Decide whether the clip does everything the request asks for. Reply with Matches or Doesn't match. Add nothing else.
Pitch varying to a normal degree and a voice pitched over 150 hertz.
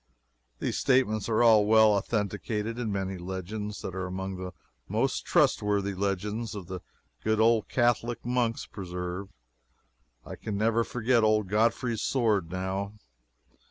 Doesn't match